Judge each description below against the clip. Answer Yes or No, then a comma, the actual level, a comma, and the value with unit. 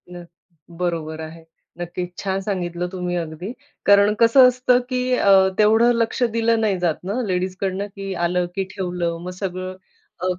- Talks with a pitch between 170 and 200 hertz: Yes, medium, 185 Hz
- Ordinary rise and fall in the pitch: Yes, average, 3.1 semitones